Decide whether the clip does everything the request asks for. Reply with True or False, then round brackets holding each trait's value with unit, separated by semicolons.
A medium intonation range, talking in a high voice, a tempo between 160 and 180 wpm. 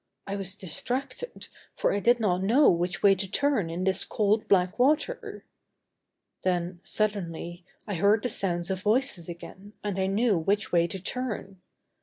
True (3.4 semitones; 195 Hz; 165 wpm)